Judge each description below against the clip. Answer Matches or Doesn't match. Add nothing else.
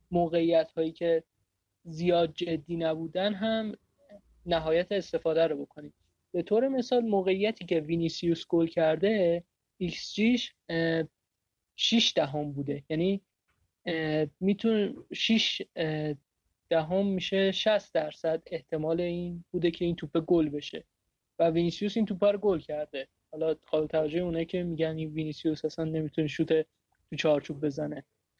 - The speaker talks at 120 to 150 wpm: Matches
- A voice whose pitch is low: Doesn't match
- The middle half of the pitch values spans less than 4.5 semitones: Matches